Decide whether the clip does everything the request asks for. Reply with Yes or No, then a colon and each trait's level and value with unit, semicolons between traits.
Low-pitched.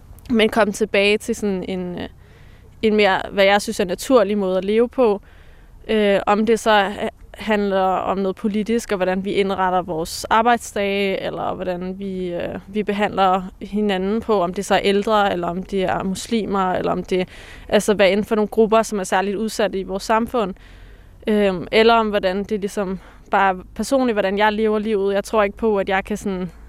No: high, 205 Hz